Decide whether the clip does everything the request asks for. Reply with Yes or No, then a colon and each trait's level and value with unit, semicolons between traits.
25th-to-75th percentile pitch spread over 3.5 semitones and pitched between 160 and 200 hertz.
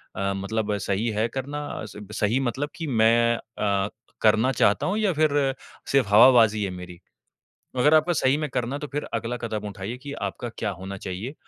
No: average, 4.9 semitones; low, 115 Hz